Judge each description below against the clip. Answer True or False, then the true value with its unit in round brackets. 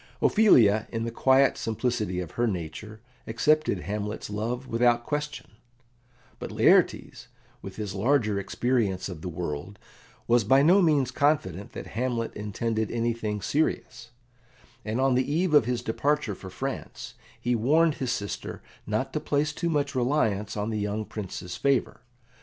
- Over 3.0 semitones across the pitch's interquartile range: True (4.6 semitones)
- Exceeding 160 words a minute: False (150 wpm)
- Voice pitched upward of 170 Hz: False (115 Hz)